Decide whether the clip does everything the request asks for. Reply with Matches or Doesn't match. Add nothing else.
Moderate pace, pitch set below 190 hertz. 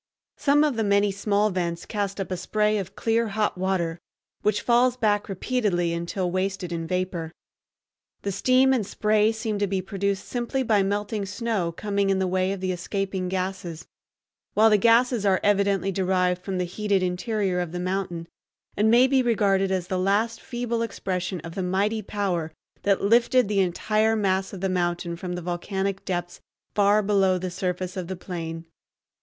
Doesn't match